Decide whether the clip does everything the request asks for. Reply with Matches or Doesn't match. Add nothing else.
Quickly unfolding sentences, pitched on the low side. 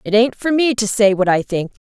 Doesn't match